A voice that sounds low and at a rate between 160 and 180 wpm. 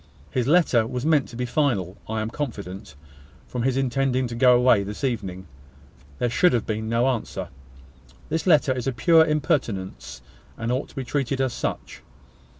Yes: low, 125 Hz; average, 175 wpm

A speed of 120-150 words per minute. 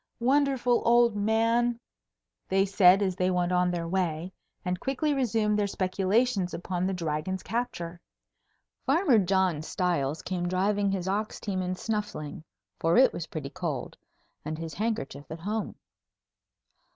Yes: average, 140 wpm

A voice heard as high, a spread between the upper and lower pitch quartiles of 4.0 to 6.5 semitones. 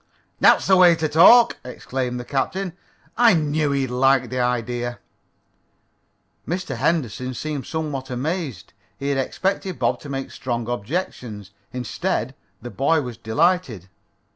No: low, 135 Hz; average, 4.9 semitones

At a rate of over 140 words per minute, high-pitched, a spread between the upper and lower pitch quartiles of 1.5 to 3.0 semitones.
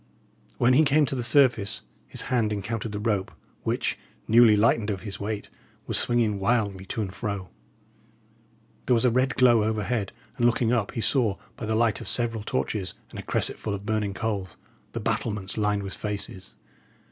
No: average, 180 wpm; low, 110 Hz; average, 2.7 semitones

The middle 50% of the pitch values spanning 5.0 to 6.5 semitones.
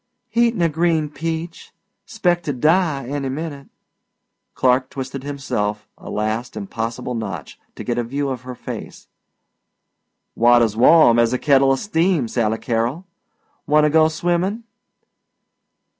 Yes: average, 5.3 semitones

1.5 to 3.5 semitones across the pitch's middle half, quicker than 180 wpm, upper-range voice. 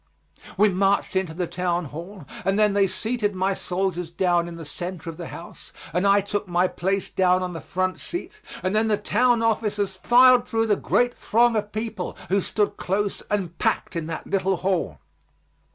Yes: average, 2.8 semitones; average, 190 wpm; high, 195 Hz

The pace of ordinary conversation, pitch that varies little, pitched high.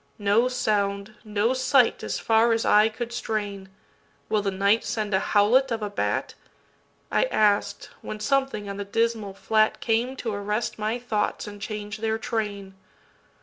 Yes: average, 145 wpm; narrow, 2.1 semitones; high, 215 Hz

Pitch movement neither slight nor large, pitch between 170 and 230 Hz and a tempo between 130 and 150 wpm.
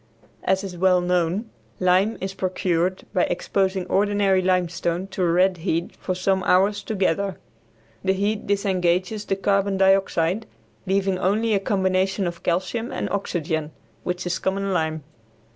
No: narrow, 1.7 semitones; high, 190 Hz; average, 145 wpm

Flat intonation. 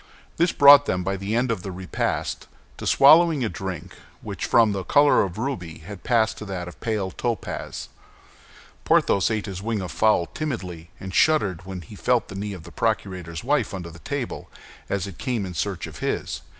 No: average, 4.4 semitones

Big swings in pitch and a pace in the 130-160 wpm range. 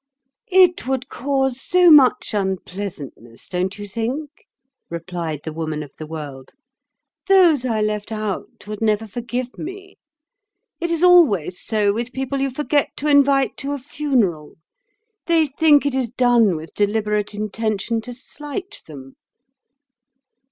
Yes: wide, 6.5 semitones; slow, 135 wpm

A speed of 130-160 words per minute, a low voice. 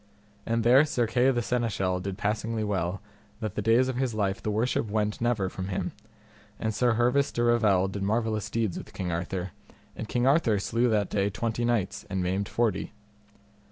No: average, 190 wpm; low, 110 Hz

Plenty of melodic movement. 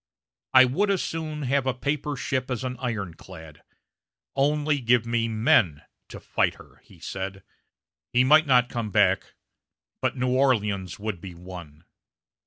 Yes: wide, 6.0 semitones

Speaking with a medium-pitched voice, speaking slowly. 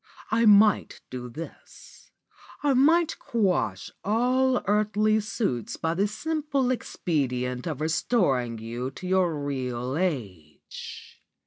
Yes: medium, 180 Hz; slow, 115 wpm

